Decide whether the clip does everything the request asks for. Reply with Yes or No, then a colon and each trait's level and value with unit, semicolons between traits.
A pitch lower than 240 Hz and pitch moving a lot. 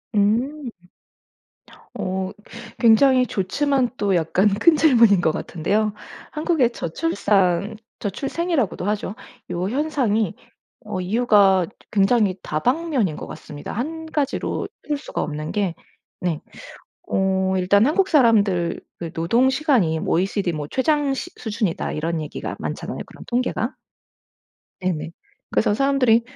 Yes: high, 210 Hz; wide, 6.3 semitones